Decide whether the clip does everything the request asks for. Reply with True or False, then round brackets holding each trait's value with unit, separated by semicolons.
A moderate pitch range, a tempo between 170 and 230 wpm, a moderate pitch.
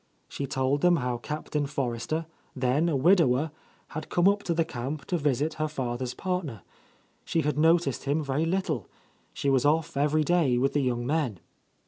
True (3.8 semitones; 180 wpm; 145 Hz)